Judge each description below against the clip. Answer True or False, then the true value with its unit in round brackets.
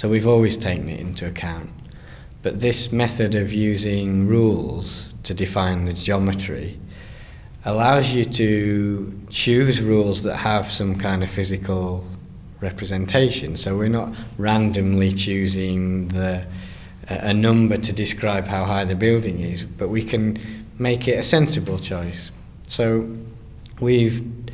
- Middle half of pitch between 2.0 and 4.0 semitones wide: True (3.1 semitones)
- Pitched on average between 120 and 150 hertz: False (105 Hz)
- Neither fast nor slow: False (130 wpm)